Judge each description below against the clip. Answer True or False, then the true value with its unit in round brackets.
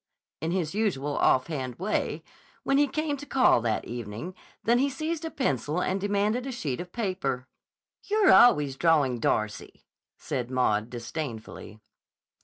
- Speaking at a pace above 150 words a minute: False (145 wpm)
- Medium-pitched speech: True (165 Hz)